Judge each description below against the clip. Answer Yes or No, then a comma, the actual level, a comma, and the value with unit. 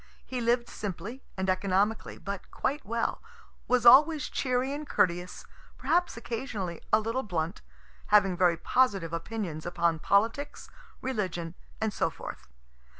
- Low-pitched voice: No, high, 210 Hz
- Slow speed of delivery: Yes, slow, 130 wpm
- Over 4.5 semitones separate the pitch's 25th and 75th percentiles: Yes, wide, 5.6 semitones